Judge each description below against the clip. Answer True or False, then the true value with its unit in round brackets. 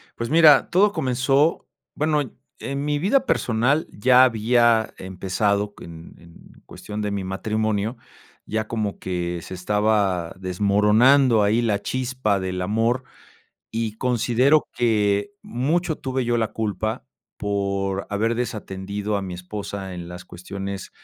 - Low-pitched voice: True (110 Hz)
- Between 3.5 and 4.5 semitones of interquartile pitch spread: True (4.2 semitones)